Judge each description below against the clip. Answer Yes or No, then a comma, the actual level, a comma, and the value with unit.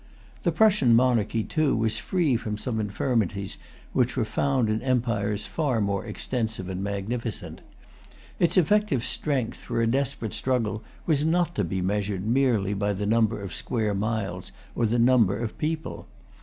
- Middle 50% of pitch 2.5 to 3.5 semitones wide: No, average, 4.1 semitones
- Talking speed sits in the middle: Yes, average, 155 wpm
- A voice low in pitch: Yes, low, 115 Hz